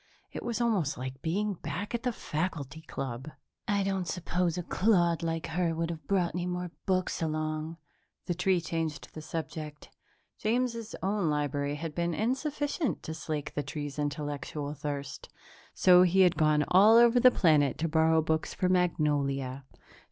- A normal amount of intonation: Yes, average, 3.9 semitones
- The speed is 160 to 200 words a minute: Yes, average, 165 wpm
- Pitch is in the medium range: Yes, medium, 165 Hz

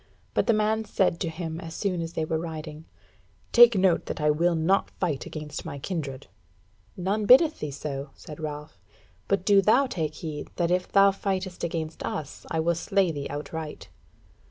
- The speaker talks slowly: No, average, 180 wpm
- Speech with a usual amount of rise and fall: Yes, average, 4.0 semitones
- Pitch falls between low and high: Yes, medium, 165 Hz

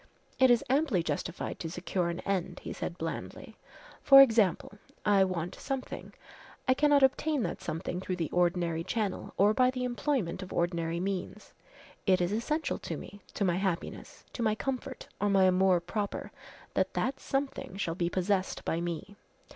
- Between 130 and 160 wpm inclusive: No, average, 170 wpm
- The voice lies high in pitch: Yes, high, 195 Hz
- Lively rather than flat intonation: Yes, wide, 6.1 semitones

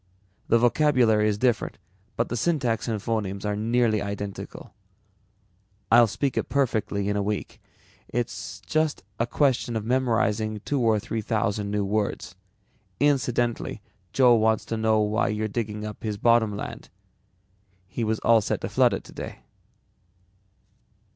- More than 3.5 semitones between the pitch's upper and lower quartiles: No, narrow, 2.5 semitones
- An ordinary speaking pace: Yes, average, 145 wpm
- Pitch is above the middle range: No, low, 110 Hz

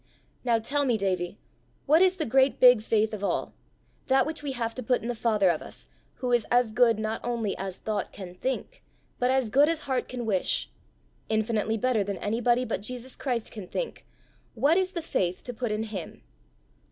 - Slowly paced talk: No, average, 200 wpm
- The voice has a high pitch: Yes, high, 235 Hz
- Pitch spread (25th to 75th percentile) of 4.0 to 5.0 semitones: No, average, 3.4 semitones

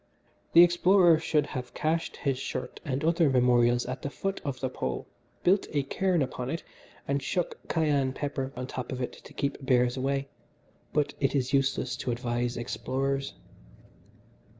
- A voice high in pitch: No, low, 135 Hz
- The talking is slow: No, average, 165 wpm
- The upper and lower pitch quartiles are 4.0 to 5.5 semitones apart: No, average, 3.2 semitones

